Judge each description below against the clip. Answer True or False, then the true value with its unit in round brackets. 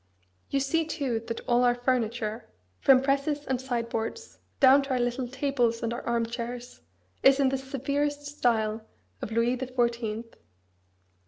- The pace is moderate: True (155 wpm)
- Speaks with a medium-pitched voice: False (245 Hz)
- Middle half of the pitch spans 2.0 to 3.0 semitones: True (2.7 semitones)